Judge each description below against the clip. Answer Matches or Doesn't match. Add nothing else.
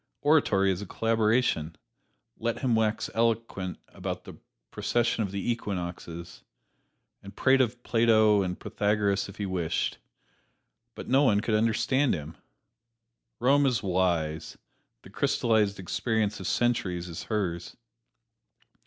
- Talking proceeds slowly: Matches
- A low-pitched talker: Matches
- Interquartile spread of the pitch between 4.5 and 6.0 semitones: Doesn't match